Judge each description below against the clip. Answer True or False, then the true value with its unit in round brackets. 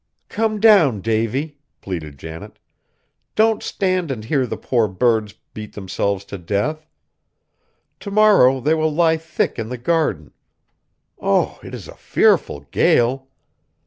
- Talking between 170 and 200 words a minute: False (135 wpm)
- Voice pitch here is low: True (130 Hz)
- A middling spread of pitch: False (7.4 semitones)